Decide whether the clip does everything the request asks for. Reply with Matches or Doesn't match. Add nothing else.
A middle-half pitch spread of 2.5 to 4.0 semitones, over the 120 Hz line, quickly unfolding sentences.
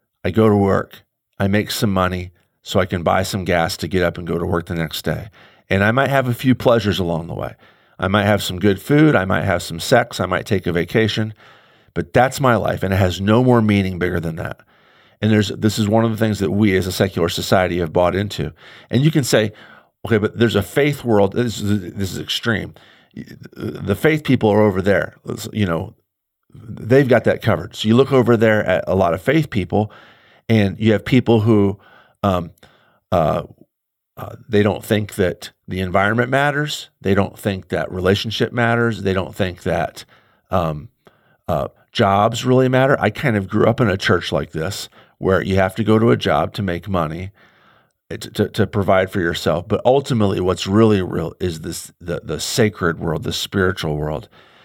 Doesn't match